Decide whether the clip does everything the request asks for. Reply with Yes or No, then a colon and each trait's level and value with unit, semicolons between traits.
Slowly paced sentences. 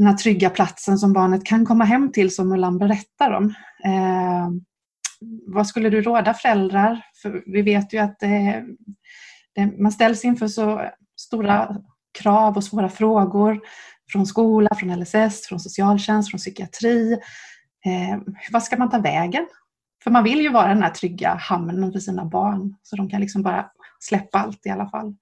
No: average, 170 wpm